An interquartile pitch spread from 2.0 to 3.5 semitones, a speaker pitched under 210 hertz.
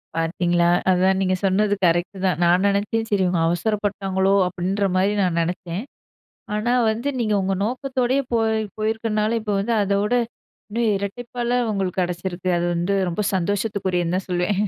Yes: average, 3.2 semitones; high, 195 Hz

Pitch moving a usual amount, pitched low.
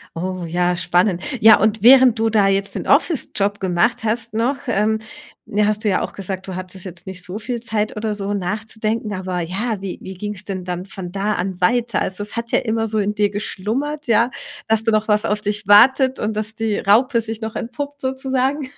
No: average, 3.0 semitones; high, 210 Hz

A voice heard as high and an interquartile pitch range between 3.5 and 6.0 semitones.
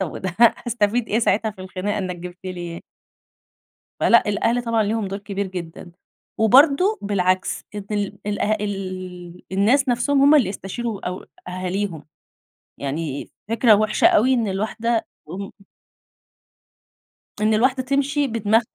Yes: high, 205 Hz; average, 3.9 semitones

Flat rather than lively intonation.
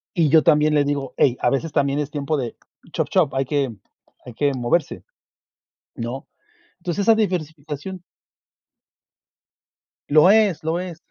No: average, 3.7 semitones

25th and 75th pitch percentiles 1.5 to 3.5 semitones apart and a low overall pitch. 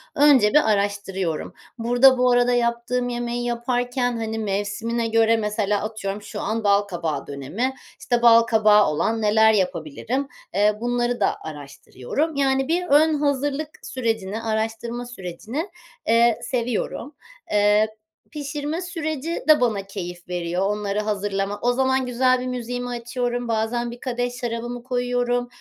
No: average, 3.1 semitones; high, 235 Hz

